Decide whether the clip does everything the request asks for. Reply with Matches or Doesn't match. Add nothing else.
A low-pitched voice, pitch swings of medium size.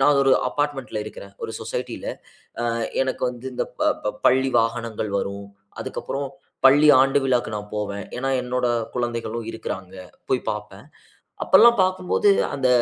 Matches